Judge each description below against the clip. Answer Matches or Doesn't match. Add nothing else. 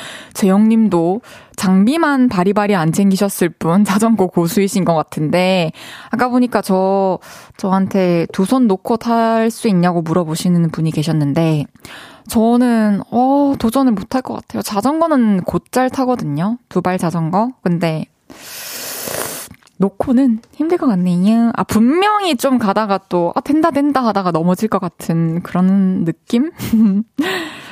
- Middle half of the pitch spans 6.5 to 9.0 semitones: Doesn't match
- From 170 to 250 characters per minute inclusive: Doesn't match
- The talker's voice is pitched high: Matches